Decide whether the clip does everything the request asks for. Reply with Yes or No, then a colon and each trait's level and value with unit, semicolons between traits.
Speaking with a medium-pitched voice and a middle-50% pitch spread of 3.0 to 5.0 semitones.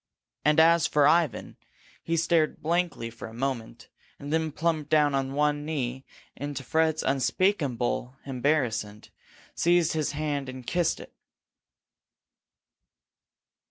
Yes: medium, 145 Hz; average, 3.6 semitones